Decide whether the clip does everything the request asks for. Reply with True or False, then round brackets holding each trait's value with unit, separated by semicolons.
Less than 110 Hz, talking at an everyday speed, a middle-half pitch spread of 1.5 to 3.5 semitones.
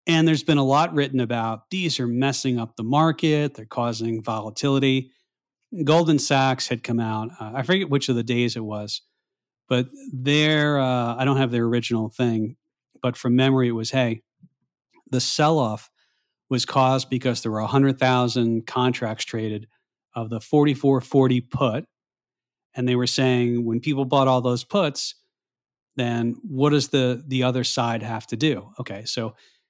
False (125 Hz; 165 wpm; 2.9 semitones)